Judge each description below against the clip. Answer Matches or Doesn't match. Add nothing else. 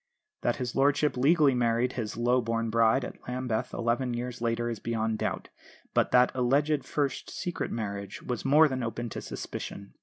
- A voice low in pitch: Matches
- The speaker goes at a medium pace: Matches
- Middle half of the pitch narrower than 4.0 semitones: Matches